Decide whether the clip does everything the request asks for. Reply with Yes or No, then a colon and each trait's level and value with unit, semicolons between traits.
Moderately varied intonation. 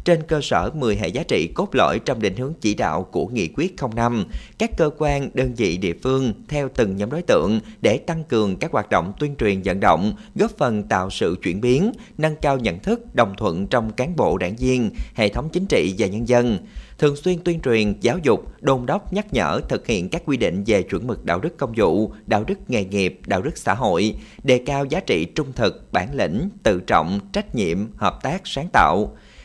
No: wide, 7.5 semitones